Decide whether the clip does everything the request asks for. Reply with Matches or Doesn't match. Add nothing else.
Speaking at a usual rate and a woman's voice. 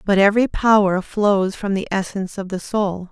Matches